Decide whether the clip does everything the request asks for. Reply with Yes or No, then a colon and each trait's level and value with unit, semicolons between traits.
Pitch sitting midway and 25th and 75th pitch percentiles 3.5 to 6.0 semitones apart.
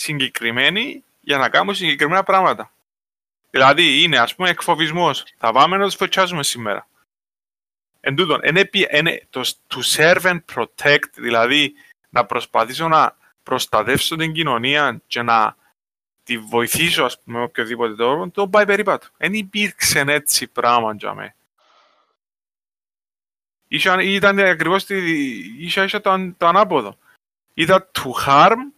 Yes: medium, 170 Hz; average, 5.1 semitones